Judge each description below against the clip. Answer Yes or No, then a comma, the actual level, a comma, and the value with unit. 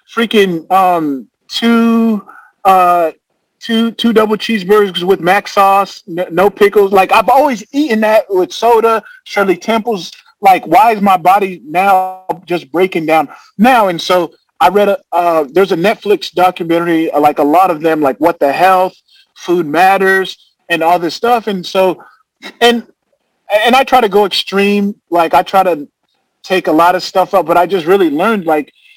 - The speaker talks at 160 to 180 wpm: Yes, average, 170 wpm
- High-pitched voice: Yes, high, 195 Hz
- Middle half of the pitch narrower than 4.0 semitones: No, average, 4.3 semitones